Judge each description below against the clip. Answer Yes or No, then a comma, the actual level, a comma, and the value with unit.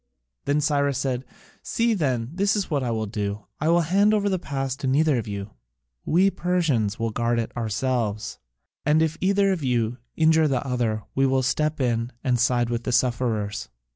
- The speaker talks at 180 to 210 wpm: Yes, average, 190 wpm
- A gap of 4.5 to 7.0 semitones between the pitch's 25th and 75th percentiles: Yes, average, 5.3 semitones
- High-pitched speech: No, low, 130 Hz